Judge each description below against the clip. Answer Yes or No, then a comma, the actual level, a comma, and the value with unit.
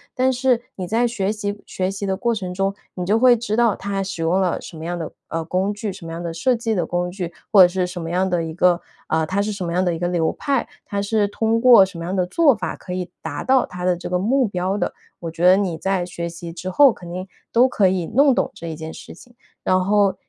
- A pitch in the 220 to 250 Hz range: No, high, 190 Hz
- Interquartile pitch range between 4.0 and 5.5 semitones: No, average, 3.3 semitones